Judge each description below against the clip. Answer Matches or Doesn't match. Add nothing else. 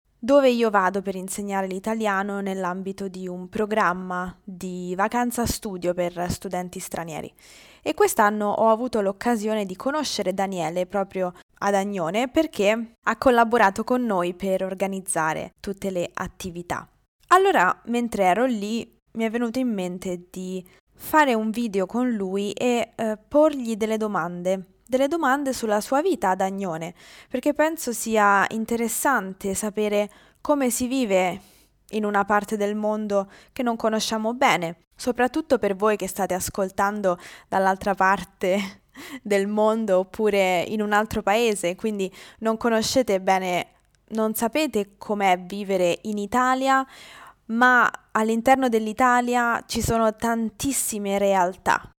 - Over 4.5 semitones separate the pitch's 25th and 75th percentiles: Doesn't match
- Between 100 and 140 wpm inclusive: Matches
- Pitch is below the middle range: Doesn't match